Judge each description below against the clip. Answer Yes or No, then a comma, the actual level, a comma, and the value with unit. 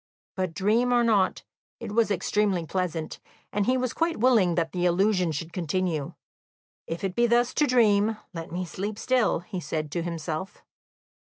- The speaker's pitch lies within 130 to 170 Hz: No, high, 190 Hz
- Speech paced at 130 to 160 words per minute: No, average, 170 wpm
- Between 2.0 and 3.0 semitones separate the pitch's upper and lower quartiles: No, average, 4.8 semitones